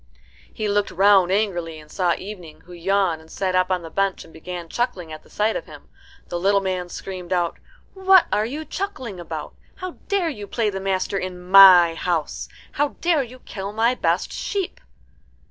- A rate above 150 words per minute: Yes, average, 190 wpm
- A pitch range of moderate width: Yes, average, 3.8 semitones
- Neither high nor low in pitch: No, high, 195 Hz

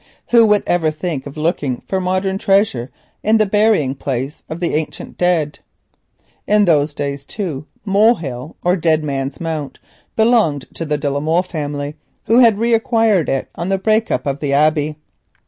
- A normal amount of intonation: No, wide, 5.8 semitones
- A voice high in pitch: No, medium, 160 Hz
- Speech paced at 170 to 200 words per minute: Yes, average, 175 wpm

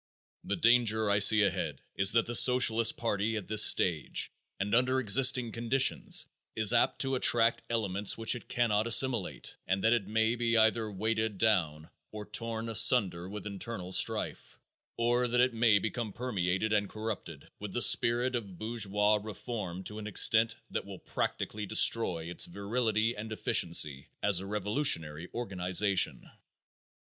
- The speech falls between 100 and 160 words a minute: Yes, average, 155 wpm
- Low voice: Yes, low, 110 Hz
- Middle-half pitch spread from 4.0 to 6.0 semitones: No, average, 2.7 semitones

